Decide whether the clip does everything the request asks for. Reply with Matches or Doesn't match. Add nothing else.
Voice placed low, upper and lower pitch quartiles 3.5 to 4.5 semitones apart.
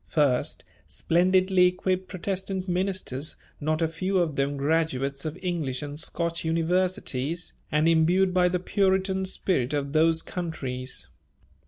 Doesn't match